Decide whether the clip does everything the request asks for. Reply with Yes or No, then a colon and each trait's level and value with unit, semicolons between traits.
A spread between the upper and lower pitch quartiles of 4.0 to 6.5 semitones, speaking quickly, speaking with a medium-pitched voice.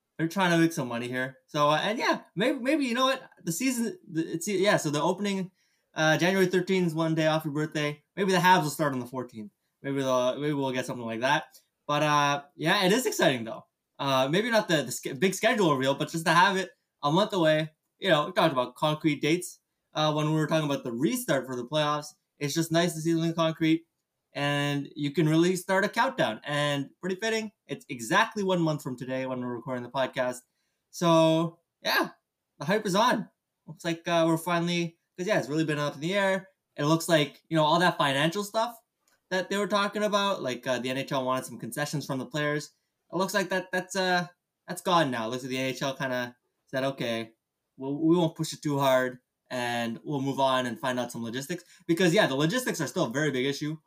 Yes: average, 4.6 semitones; fast, 225 wpm; medium, 155 Hz